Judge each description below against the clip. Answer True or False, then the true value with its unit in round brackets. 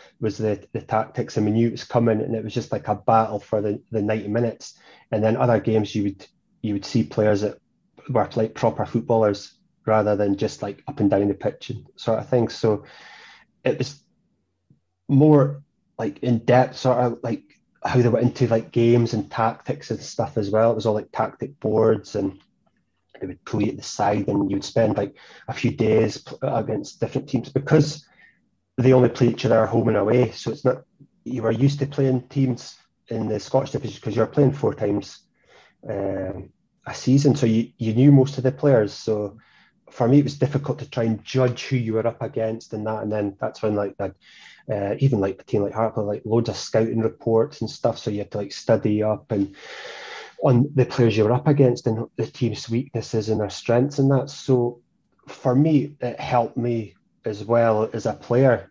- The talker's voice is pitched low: True (115 Hz)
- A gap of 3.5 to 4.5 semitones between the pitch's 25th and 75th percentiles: False (3.0 semitones)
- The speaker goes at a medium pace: False (210 wpm)